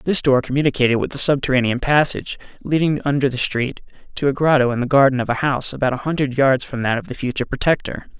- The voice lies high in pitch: No, low, 135 Hz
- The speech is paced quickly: Yes, fast, 220 wpm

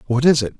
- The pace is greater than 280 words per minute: Yes, fast, 305 wpm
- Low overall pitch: Yes, low, 125 Hz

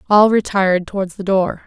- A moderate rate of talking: Yes, average, 180 wpm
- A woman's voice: Yes, female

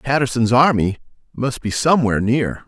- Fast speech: No, slow, 135 wpm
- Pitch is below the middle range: Yes, low, 125 Hz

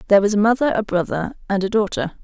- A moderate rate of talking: No, fast, 240 wpm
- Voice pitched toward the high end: Yes, high, 205 Hz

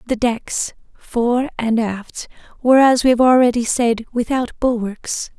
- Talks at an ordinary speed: Yes, average, 145 wpm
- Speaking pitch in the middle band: No, high, 240 Hz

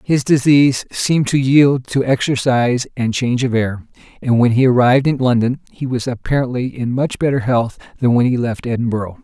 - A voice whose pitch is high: No, low, 125 Hz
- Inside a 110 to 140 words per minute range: No, average, 190 wpm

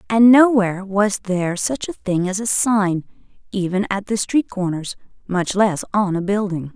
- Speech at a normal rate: Yes, average, 180 wpm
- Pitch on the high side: Yes, high, 200 Hz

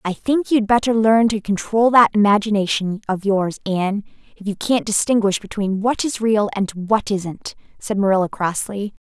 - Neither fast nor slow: Yes, average, 170 wpm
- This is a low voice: No, high, 210 Hz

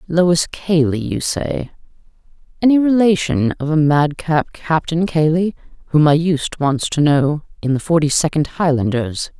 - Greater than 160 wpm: No, average, 140 wpm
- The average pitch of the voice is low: No, medium, 155 Hz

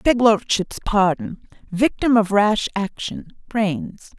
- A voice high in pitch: Yes, high, 205 Hz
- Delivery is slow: Yes, slow, 70 wpm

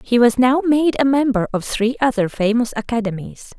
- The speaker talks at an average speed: Yes, average, 185 wpm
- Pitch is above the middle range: Yes, high, 240 Hz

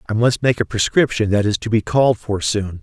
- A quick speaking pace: Yes, fast, 255 wpm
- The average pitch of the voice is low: Yes, low, 110 Hz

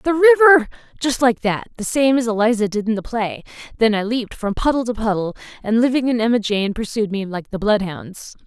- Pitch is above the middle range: Yes, high, 225 Hz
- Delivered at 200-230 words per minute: Yes, fast, 205 wpm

